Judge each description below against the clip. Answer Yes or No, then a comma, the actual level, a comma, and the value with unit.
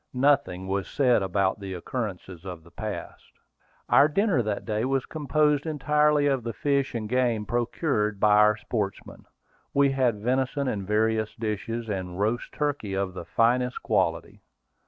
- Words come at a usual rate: Yes, average, 155 wpm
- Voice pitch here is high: No, low, 115 Hz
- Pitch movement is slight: No, average, 4.9 semitones